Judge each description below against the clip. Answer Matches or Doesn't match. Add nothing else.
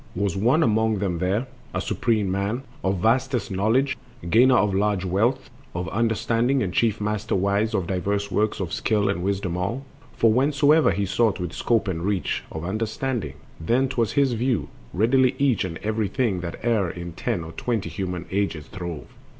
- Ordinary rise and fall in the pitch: Matches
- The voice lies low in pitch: Matches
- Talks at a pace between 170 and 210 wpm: Matches